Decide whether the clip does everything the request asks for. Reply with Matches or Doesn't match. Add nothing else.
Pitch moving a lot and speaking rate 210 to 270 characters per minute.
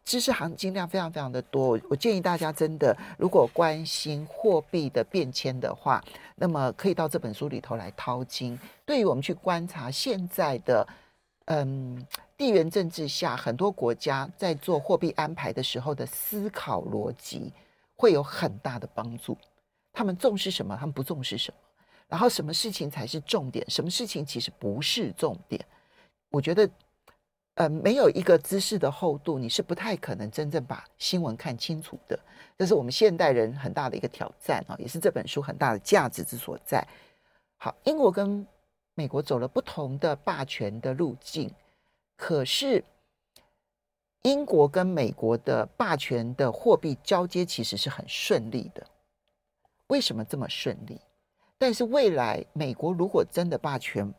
Matches